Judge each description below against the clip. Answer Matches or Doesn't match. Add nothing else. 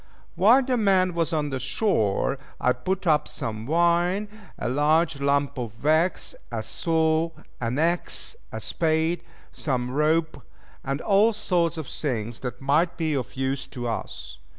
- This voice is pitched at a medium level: Matches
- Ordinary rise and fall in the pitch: Matches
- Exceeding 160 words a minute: Doesn't match